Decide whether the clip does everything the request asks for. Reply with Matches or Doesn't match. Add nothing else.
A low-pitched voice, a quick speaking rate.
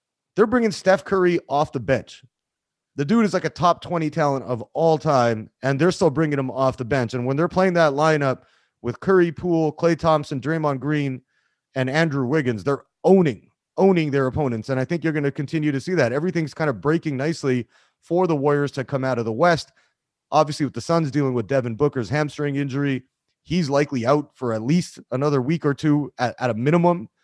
Doesn't match